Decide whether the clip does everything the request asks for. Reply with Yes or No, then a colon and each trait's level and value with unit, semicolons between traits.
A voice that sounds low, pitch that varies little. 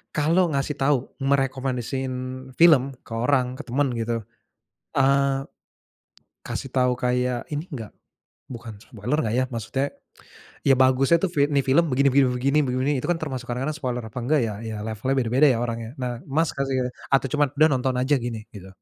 Yes: low, 130 Hz; narrow, 2.3 semitones